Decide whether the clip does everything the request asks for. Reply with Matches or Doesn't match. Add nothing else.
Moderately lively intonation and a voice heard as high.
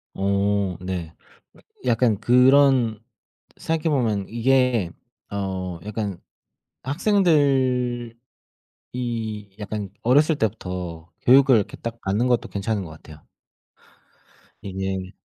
Doesn't match